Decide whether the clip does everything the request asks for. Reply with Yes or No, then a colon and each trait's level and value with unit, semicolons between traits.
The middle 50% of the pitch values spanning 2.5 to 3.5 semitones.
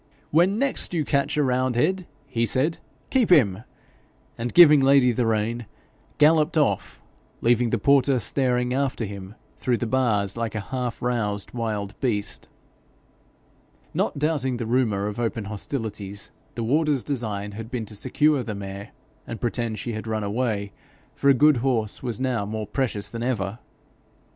No: average, 4.0 semitones